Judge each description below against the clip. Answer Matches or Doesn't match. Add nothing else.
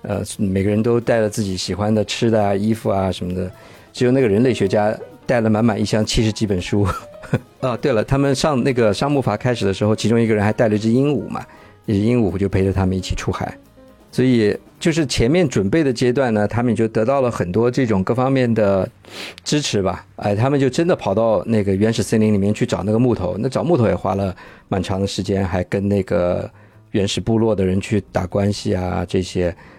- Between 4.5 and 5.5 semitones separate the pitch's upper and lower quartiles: Doesn't match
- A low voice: Matches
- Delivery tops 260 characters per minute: Matches